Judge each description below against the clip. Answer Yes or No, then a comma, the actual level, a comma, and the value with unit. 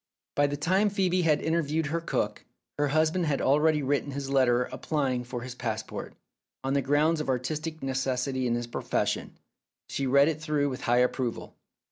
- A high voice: No, medium, 140 Hz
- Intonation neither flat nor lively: Yes, average, 3.4 semitones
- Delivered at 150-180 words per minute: Yes, average, 175 wpm